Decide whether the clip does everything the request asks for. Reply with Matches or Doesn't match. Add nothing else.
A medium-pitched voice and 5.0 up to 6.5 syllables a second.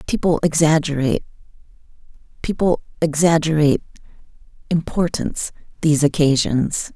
Matches